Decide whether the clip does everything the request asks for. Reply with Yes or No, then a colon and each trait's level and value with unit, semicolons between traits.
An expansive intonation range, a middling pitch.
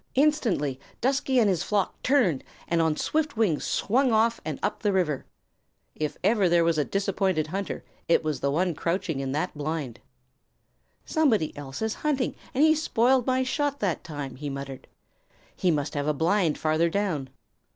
Yes: wide, 7.3 semitones; medium, 180 Hz